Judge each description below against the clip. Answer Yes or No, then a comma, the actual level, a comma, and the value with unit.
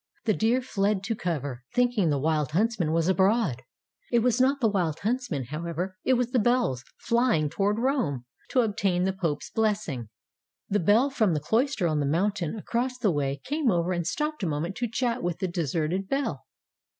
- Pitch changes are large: Yes, wide, 6.7 semitones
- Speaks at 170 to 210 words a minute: Yes, average, 190 wpm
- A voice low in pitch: No, high, 195 Hz